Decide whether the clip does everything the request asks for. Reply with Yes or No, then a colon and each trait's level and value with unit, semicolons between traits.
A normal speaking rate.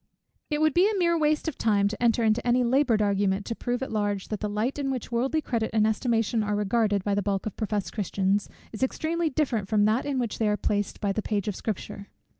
No: fast, 235 wpm